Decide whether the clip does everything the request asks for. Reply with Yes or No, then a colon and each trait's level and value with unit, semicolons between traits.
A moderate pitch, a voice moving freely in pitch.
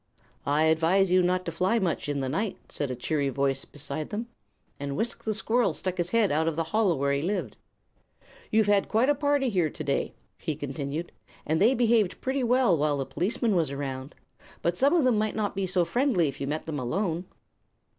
Yes: medium, 175 Hz; wide, 6.9 semitones